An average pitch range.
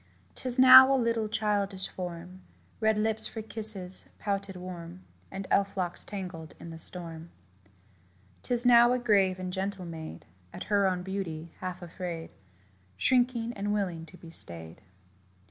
Yes: average, 3.7 semitones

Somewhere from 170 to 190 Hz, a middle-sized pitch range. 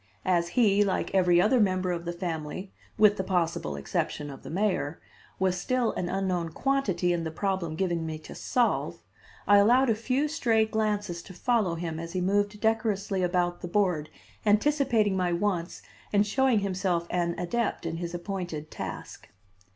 Yes: medium, 185 Hz; average, 3.6 semitones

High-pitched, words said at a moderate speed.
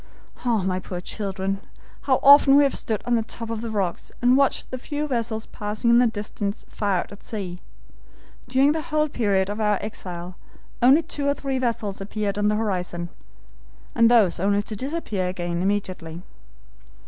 Yes: high, 215 Hz; average, 180 wpm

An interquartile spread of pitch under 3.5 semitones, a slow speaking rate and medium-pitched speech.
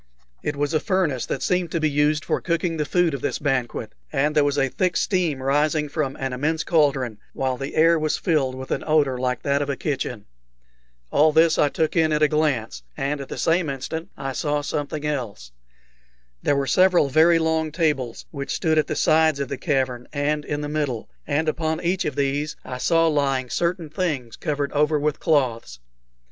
No: average, 2.7 semitones; fast, 205 wpm; medium, 150 Hz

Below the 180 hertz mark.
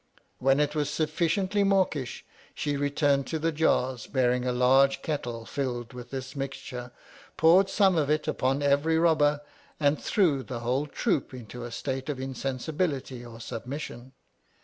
Yes: medium, 140 Hz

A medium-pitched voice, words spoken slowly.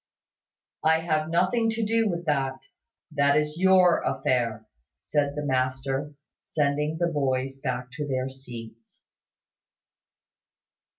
Yes: medium, 145 Hz; slow, 115 wpm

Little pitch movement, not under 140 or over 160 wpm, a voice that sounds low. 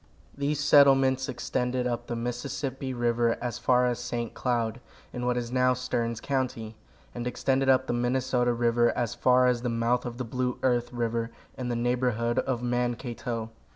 No: narrow, 1.3 semitones; average, 170 wpm; low, 125 Hz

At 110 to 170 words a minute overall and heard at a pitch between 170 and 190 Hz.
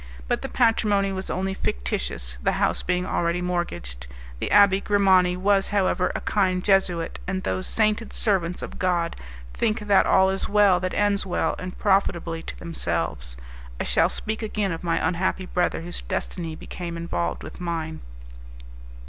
Yes: average, 160 wpm; medium, 185 Hz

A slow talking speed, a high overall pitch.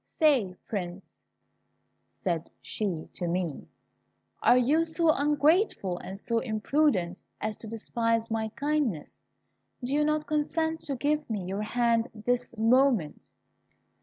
Yes: slow, 125 wpm; high, 230 Hz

